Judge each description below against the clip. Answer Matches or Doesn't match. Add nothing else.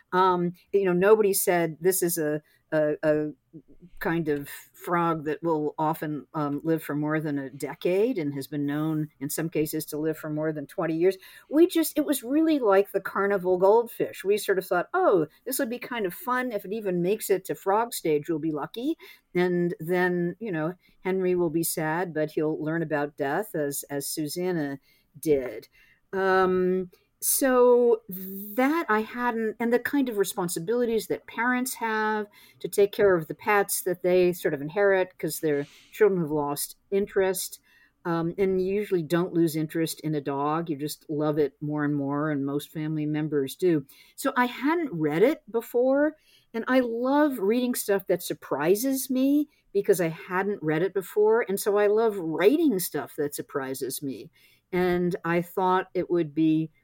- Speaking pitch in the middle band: Matches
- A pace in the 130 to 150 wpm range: Doesn't match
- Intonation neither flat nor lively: Doesn't match